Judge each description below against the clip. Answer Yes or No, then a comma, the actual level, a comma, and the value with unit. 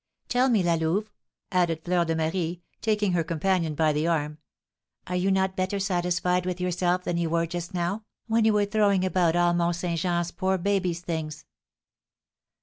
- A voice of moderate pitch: Yes, medium, 175 Hz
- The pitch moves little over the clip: Yes, narrow, 2.2 semitones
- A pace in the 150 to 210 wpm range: Yes, average, 180 wpm